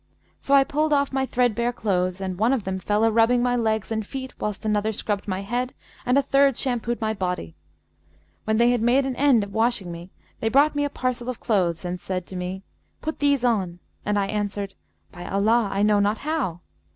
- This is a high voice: Yes, high, 220 Hz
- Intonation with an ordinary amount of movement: Yes, average, 4.3 semitones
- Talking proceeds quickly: Yes, fast, 215 wpm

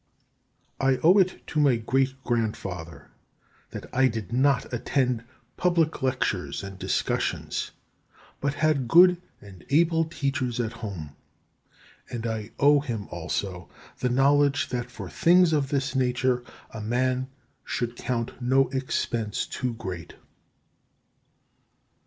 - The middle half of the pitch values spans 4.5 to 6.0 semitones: No, average, 3.7 semitones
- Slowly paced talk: Yes, slow, 125 wpm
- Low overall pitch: Yes, low, 130 Hz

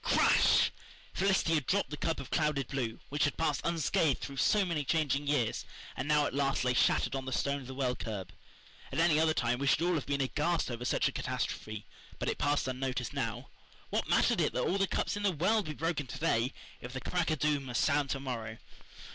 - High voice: No, medium, 145 Hz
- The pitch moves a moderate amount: Yes, average, 3.6 semitones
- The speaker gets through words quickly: Yes, fast, 230 wpm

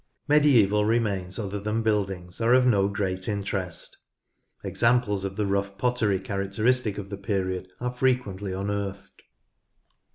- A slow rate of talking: Yes, slow, 130 wpm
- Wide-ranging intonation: No, average, 2.8 semitones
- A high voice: No, low, 100 Hz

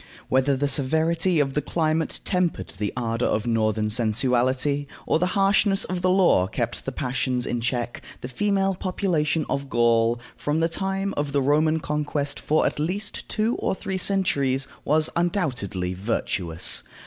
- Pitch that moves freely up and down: Yes, wide, 6.5 semitones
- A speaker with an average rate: Yes, average, 160 wpm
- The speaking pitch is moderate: Yes, medium, 145 Hz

